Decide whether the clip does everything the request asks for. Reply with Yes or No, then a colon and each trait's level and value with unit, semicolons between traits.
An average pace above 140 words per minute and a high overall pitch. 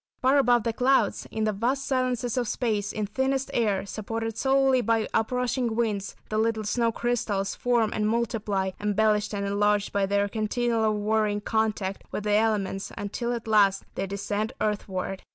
Yes: average, 170 wpm; high, 220 Hz